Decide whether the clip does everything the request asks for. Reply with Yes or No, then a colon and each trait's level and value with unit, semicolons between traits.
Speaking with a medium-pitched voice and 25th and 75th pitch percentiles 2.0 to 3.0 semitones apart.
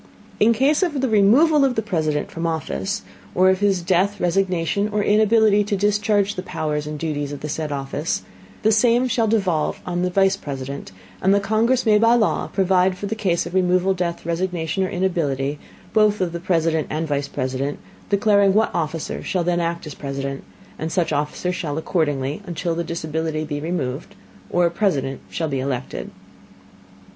No: medium, 180 Hz; average, 4.8 semitones